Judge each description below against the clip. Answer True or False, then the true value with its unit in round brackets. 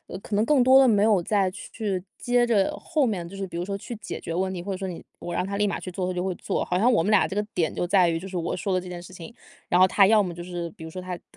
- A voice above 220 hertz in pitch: False (190 Hz)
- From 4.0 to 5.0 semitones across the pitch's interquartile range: False (2.7 semitones)